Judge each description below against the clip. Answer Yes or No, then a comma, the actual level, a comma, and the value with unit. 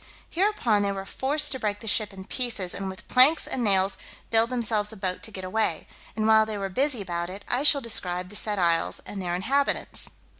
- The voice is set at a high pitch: Yes, high, 210 Hz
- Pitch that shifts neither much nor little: Yes, average, 4.3 semitones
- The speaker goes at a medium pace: No, fast, 220 wpm